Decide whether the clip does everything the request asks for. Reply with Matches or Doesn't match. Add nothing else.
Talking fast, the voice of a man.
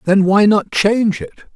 Doesn't match